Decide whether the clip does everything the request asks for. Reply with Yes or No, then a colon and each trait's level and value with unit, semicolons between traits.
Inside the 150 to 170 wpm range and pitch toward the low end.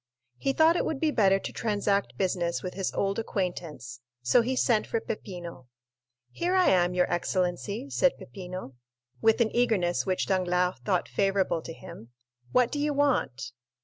No: average, 165 wpm; high, 195 Hz